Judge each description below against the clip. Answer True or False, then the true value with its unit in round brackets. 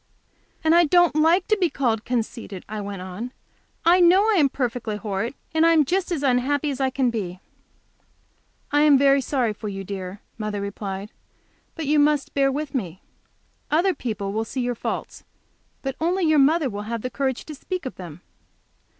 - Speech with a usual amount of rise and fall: False (6.4 semitones)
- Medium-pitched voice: False (265 Hz)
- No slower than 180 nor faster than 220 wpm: True (190 wpm)